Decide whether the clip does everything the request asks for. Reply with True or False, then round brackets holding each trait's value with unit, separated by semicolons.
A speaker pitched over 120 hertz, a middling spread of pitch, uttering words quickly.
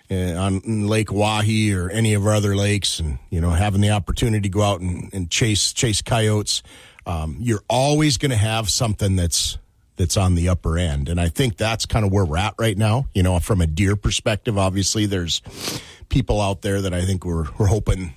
False (100 Hz; 3.2 semitones; 210 wpm)